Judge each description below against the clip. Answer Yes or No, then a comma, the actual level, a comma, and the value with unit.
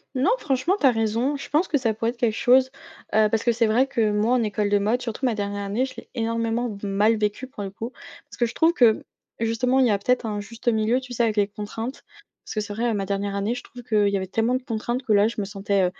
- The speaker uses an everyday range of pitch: Yes, average, 3.1 semitones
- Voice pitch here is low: No, high, 225 Hz